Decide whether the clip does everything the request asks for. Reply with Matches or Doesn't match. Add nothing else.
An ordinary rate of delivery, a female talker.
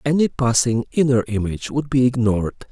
Doesn't match